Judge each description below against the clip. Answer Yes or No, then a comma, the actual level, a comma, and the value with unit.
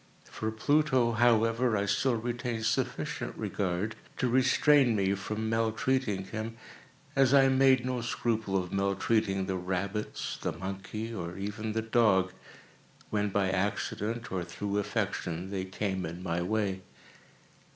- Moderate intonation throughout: Yes, average, 3.4 semitones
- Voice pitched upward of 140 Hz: No, low, 105 Hz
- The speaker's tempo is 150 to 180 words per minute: No, slow, 135 wpm